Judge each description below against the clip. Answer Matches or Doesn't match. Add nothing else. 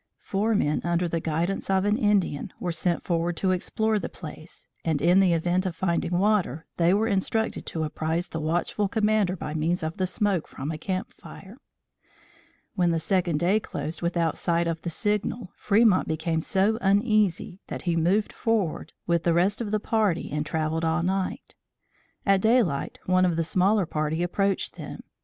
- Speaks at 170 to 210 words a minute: Matches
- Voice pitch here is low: Doesn't match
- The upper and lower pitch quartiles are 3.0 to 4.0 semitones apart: Matches